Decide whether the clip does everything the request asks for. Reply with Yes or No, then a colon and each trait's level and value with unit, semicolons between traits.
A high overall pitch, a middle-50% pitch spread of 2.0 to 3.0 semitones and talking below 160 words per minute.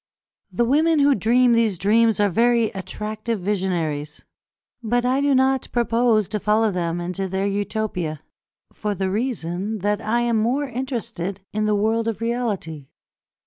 No: high, 215 Hz; average, 3.8 semitones; average, 150 wpm